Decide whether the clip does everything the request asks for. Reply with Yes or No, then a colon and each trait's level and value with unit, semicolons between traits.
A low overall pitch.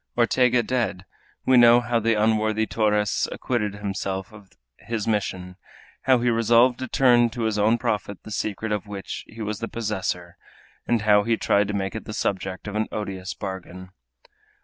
Yes: low, 105 Hz